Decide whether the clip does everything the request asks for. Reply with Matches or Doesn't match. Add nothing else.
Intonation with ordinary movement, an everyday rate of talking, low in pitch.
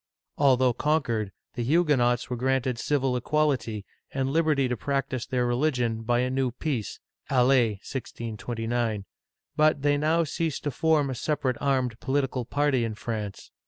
Matches